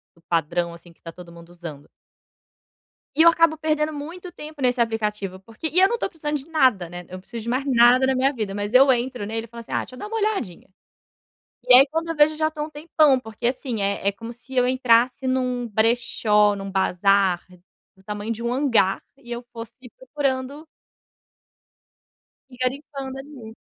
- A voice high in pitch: Yes, high, 245 Hz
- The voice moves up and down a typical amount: No, wide, 5.7 semitones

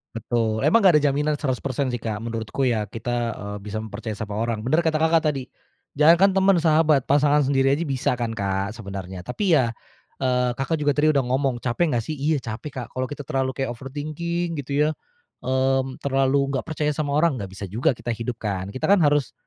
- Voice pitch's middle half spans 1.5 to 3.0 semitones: No, average, 4.7 semitones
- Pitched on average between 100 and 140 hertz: Yes, low, 135 Hz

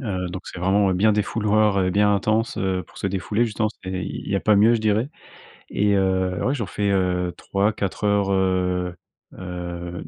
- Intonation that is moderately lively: No, narrow, 2.3 semitones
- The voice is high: No, low, 100 Hz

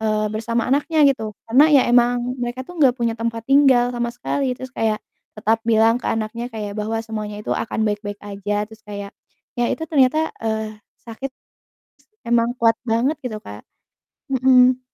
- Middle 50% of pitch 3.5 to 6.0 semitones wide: No, average, 2.8 semitones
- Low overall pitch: No, high, 235 Hz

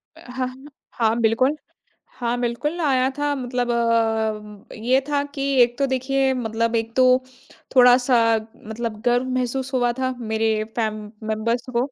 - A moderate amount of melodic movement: No, narrow, 2.2 semitones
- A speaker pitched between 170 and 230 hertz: No, high, 245 Hz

